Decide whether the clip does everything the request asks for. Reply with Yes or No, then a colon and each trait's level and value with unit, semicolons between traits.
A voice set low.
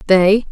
No: high, 200 Hz